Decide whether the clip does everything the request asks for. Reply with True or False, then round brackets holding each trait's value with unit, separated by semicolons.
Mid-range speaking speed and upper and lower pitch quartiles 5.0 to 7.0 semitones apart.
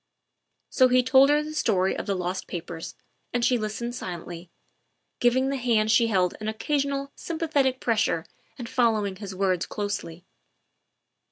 True (150 wpm; 5.5 semitones)